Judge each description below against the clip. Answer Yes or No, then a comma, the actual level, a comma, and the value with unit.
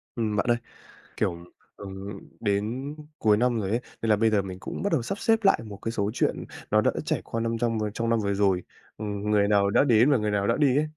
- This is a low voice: Yes, low, 110 Hz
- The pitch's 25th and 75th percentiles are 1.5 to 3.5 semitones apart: Yes, narrow, 2.6 semitones